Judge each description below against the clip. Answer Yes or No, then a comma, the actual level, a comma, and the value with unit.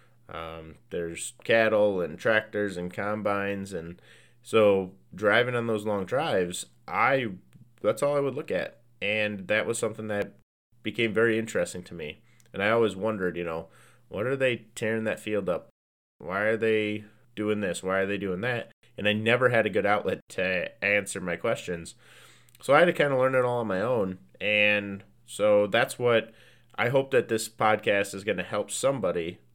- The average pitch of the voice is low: Yes, low, 105 Hz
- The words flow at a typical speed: Yes, average, 185 wpm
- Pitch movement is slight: No, average, 3.0 semitones